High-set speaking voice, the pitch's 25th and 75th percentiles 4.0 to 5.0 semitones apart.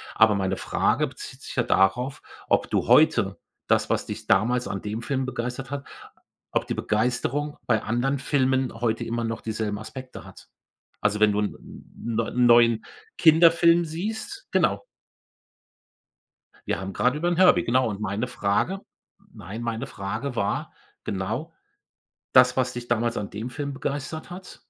No: low, 120 Hz; average, 4.3 semitones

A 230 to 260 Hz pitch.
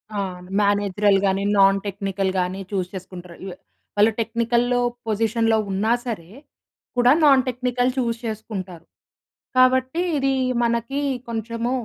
No: high, 220 Hz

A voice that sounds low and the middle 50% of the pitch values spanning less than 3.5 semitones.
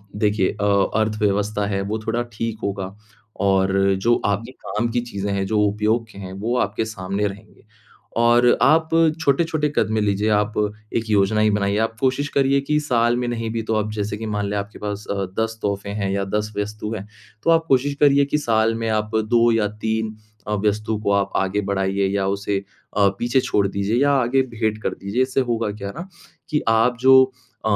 Yes: low, 110 Hz; average, 2.8 semitones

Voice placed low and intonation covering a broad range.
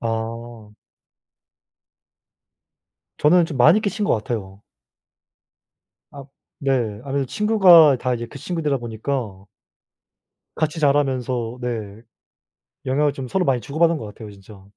No: low, 130 Hz; average, 4.9 semitones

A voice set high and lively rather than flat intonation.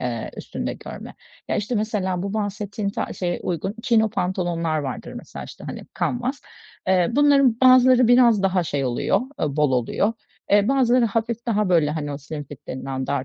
Yes: high, 200 Hz; wide, 7.1 semitones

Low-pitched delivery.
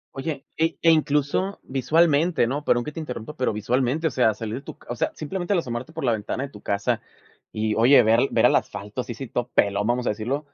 Yes: low, 130 Hz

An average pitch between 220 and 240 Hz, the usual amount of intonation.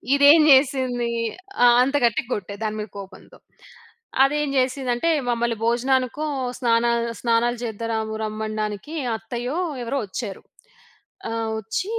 Yes: high, 235 Hz; average, 3.1 semitones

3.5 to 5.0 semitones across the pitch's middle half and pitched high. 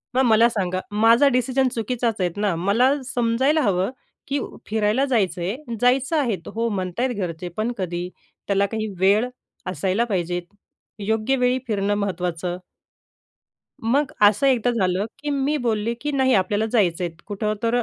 Yes: average, 4.7 semitones; high, 220 Hz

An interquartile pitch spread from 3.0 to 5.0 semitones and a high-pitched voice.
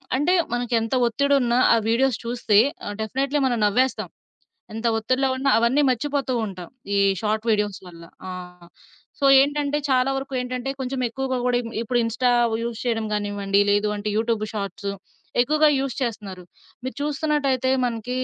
Yes: average, 3.6 semitones; high, 245 Hz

